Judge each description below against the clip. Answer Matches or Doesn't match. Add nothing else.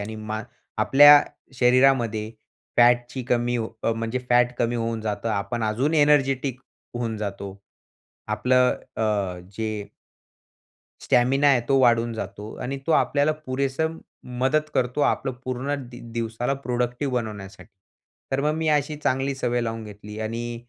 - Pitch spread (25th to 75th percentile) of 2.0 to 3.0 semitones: Doesn't match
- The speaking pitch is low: Matches